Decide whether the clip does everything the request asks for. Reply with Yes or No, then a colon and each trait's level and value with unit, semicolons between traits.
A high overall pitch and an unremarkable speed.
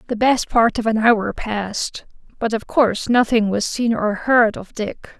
Yes: high, 225 Hz; average, 195 wpm